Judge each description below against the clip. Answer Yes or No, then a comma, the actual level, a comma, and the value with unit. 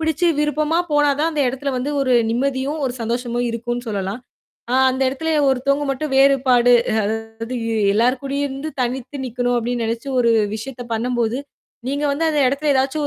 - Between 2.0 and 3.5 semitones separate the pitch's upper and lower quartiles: Yes, average, 2.9 semitones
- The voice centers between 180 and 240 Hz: No, very high, 260 Hz